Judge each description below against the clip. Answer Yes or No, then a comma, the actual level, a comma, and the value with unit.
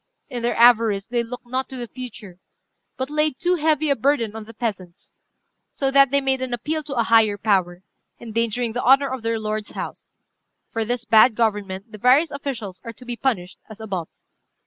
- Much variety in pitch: No, average, 3.5 semitones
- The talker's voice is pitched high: Yes, high, 235 Hz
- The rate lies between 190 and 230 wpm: Yes, average, 195 wpm